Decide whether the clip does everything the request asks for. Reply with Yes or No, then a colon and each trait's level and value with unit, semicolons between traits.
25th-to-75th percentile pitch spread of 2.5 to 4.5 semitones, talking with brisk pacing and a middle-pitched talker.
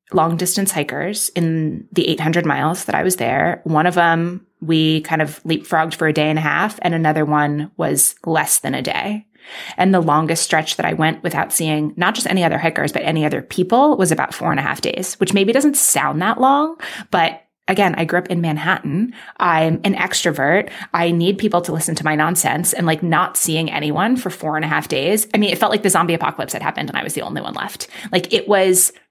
Yes: average, 3.4 semitones; fast, 230 wpm; medium, 170 Hz